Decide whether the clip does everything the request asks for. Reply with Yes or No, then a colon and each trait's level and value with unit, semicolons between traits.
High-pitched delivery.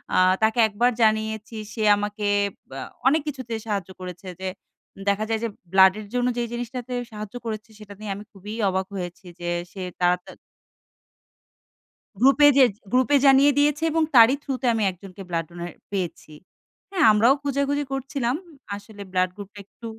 Yes: high, 220 Hz